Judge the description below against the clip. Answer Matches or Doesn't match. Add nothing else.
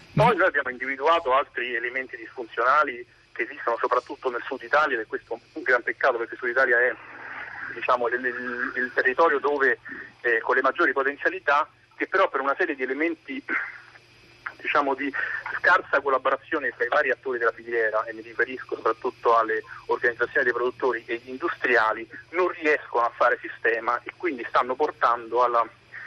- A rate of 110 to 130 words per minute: Doesn't match